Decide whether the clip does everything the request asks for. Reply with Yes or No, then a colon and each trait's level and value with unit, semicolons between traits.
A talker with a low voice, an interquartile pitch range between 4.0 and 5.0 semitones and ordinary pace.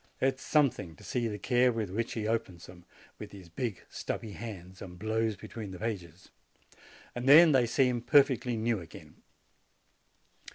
Yes: low, 110 Hz; average, 4.4 semitones; average, 165 wpm